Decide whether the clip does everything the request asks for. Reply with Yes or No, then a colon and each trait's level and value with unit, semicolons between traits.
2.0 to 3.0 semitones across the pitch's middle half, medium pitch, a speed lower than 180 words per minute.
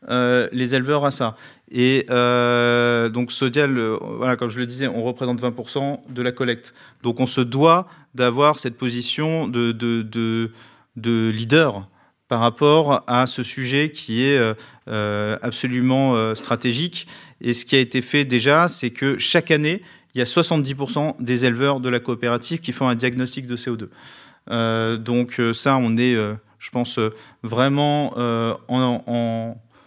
No: narrow, 2.4 semitones; low, 125 Hz; average, 165 wpm